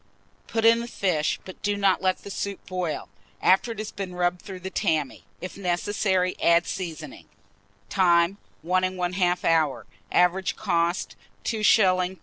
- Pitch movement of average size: No, narrow, 2.1 semitones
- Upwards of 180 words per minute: No, average, 150 wpm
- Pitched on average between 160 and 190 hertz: Yes, medium, 185 Hz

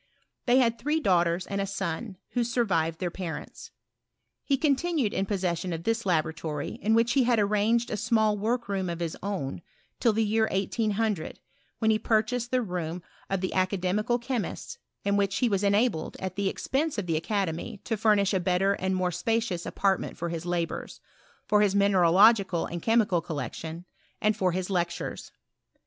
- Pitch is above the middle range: Yes, high, 200 Hz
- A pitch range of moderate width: Yes, average, 4.1 semitones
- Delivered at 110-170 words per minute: No, average, 180 wpm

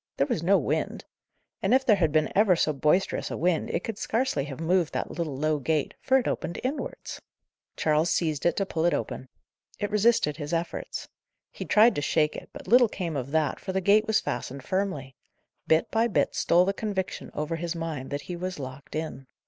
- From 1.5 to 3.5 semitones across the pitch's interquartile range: No, average, 4.8 semitones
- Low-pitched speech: No, medium, 170 Hz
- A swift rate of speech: Yes, fast, 210 wpm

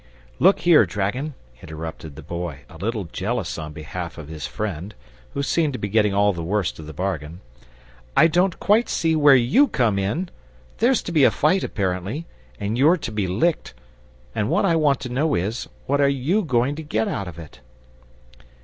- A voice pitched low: Yes, low, 110 Hz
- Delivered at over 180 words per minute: Yes, average, 195 wpm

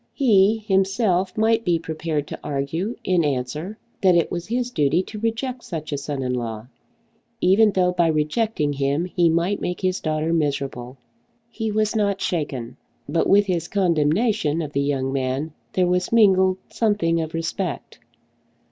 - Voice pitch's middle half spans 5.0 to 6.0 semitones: Yes, average, 5.3 semitones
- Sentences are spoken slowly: No, average, 160 wpm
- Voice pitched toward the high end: No, medium, 175 Hz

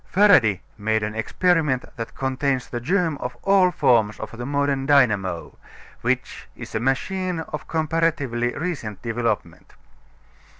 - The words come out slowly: Yes, slow, 130 wpm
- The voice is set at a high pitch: No, low, 135 Hz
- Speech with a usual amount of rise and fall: No, wide, 6.1 semitones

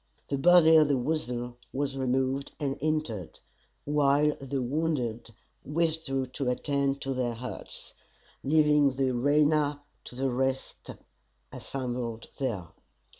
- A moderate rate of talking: No, slow, 120 wpm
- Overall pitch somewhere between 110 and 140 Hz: Yes, low, 135 Hz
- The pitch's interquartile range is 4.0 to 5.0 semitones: No, average, 2.9 semitones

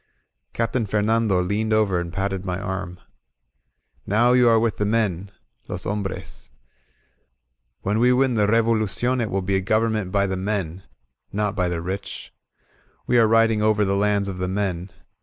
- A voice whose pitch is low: Yes, low, 105 Hz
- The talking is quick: No, average, 165 wpm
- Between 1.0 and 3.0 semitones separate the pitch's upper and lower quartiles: Yes, average, 2.7 semitones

